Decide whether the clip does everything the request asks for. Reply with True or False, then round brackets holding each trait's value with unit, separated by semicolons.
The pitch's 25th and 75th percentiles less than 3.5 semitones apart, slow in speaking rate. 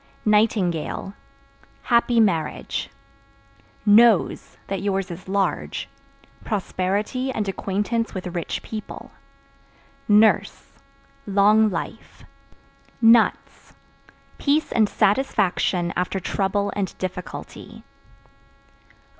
True (2.8 semitones; 80 wpm)